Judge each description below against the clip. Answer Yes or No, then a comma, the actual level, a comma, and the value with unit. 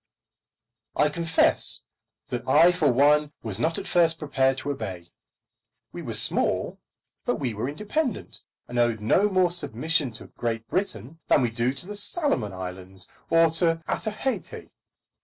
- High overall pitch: No, medium, 145 Hz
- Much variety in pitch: Yes, wide, 6.3 semitones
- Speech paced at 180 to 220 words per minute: No, average, 155 wpm